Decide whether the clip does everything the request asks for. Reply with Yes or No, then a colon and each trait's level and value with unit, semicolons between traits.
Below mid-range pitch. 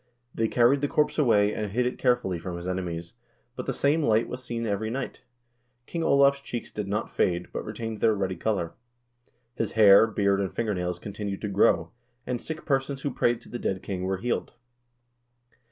Yes: low, 110 Hz